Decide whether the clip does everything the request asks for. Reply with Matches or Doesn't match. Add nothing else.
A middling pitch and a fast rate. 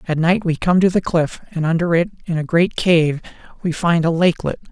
Matches